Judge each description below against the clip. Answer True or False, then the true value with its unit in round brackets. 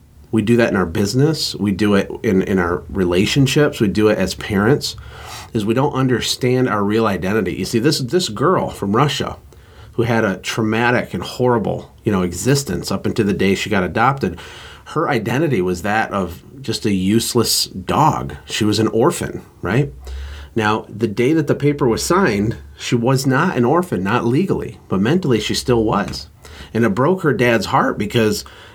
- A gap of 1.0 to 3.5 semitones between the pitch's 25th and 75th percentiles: False (4.1 semitones)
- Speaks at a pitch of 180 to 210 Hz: False (115 Hz)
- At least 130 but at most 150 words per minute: False (185 wpm)